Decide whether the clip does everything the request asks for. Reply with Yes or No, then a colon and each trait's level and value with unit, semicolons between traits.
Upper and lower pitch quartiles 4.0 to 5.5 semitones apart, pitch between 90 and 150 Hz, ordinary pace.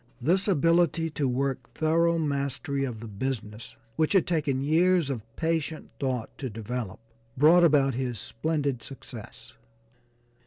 No: average, 4.6 semitones; medium, 140 Hz; slow, 130 wpm